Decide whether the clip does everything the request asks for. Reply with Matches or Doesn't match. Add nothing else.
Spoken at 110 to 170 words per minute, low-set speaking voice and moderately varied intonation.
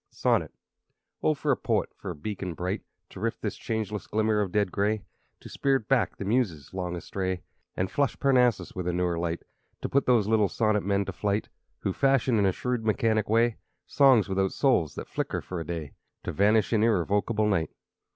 Doesn't match